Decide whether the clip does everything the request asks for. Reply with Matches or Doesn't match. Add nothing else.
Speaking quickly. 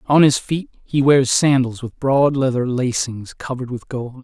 Doesn't match